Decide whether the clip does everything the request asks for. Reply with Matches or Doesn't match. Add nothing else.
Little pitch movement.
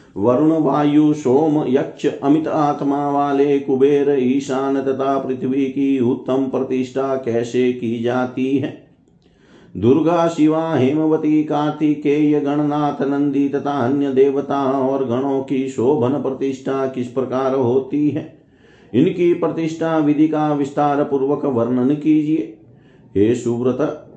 Matches